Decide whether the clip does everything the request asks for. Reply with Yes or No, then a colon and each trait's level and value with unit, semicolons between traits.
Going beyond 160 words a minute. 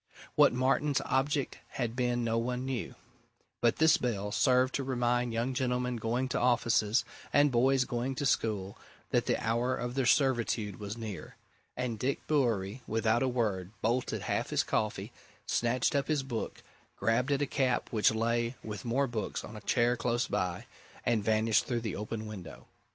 Yes: average, 175 wpm